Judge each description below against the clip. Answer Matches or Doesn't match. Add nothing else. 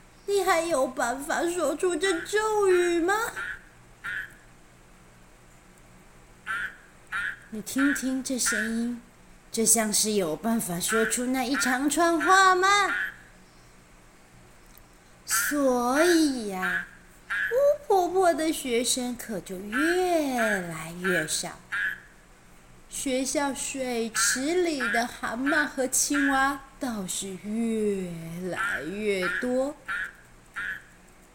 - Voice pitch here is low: Doesn't match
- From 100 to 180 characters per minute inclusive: Matches